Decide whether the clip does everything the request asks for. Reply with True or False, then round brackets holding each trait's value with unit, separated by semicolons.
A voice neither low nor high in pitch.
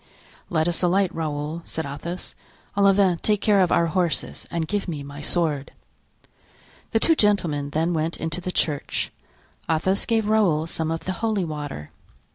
True (170 Hz)